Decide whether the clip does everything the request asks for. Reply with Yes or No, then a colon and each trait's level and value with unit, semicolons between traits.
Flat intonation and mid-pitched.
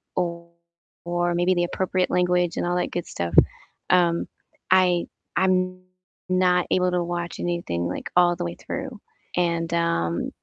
Yes: narrow, 1.2 semitones; medium, 175 Hz